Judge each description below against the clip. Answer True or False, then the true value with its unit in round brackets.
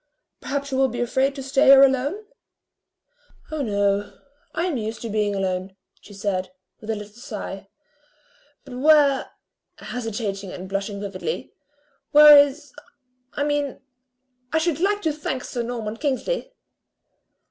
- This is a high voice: True (250 Hz)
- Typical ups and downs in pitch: False (5.8 semitones)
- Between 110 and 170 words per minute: True (140 wpm)